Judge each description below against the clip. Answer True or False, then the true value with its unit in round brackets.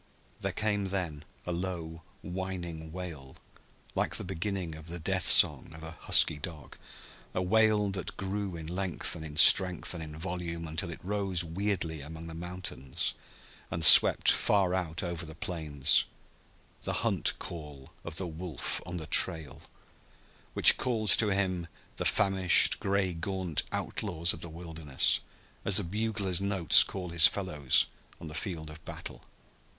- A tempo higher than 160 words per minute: False (155 wpm)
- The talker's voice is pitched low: True (85 Hz)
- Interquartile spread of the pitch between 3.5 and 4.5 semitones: False (2.9 semitones)